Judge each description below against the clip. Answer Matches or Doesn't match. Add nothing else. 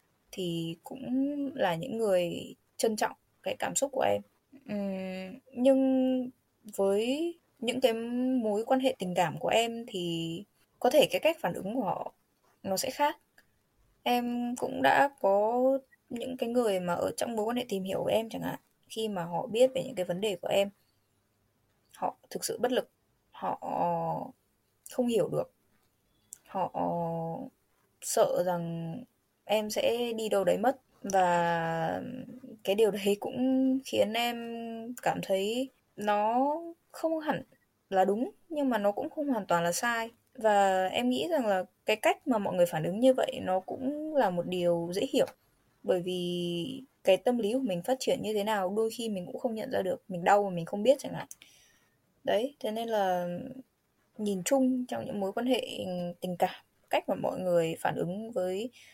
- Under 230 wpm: Matches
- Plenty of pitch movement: Matches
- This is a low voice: Doesn't match